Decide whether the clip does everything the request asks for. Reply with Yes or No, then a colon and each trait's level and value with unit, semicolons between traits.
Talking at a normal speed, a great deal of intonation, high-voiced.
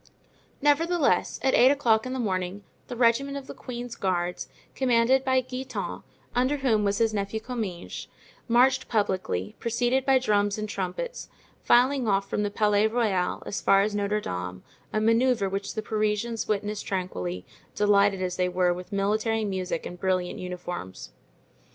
No: average, 155 wpm; average, 4.4 semitones; high, 210 Hz